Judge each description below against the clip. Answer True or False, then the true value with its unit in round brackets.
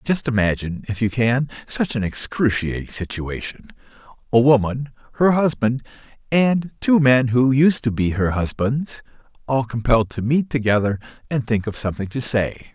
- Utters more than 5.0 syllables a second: False (4.9 syllables/s)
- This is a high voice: False (120 Hz)